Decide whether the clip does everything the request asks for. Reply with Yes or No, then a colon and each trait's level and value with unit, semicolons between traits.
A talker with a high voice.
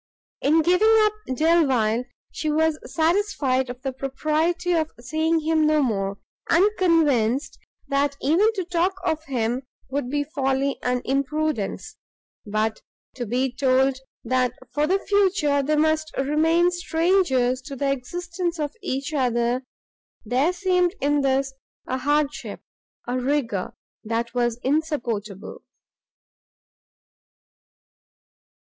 Yes: very high, 285 Hz